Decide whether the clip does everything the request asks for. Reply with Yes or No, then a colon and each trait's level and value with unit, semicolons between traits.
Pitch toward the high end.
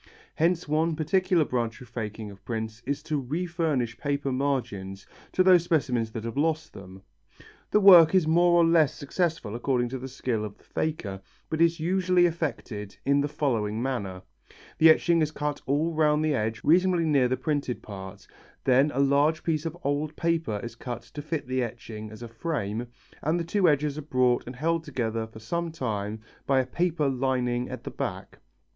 No: medium, 140 Hz